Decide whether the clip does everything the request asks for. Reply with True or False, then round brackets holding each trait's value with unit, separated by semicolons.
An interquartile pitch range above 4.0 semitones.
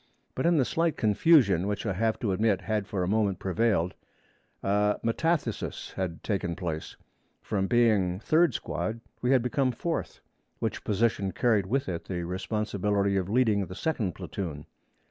False (3.7 semitones)